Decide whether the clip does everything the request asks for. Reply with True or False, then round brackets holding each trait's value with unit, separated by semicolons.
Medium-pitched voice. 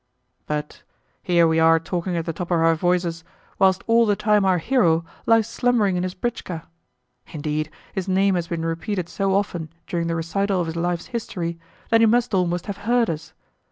True (180 Hz)